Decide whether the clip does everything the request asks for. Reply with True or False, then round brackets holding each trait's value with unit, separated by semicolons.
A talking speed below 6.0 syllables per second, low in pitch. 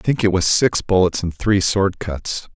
True (4.5 syllables/s; 95 Hz)